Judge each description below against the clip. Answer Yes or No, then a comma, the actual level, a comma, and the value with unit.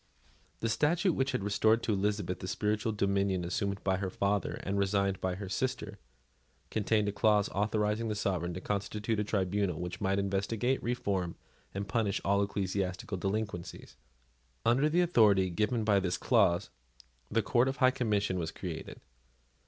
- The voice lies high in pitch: No, low, 100 Hz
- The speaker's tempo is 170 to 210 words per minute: No, average, 155 wpm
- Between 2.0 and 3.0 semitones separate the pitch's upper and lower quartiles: Yes, narrow, 2.4 semitones